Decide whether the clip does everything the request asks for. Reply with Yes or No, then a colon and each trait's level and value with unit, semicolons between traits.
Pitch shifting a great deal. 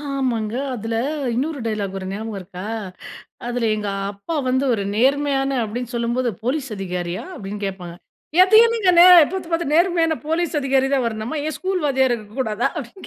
Yes: wide, 5.8 semitones